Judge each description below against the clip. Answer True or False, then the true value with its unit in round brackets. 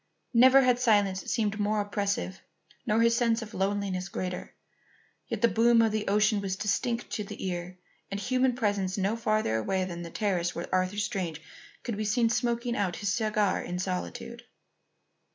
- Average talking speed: True (170 wpm)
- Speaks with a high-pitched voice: True (205 Hz)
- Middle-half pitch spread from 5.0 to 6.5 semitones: False (3.5 semitones)